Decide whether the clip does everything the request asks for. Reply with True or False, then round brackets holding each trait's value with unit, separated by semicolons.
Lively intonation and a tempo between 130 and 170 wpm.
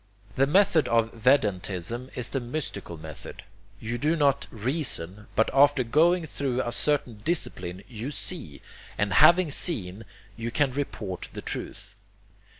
True (5.7 semitones; 140 wpm)